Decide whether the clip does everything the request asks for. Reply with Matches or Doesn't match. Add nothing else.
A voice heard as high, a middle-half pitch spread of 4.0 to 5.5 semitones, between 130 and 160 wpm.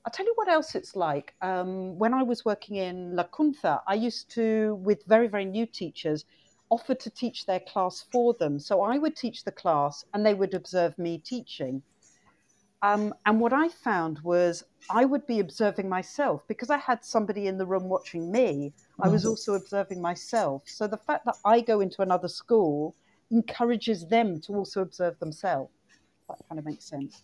Doesn't match